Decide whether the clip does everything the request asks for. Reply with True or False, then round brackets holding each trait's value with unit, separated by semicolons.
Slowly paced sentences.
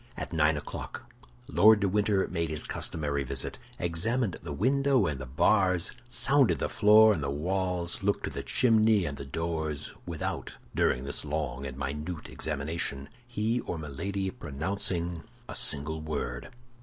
False (155 wpm)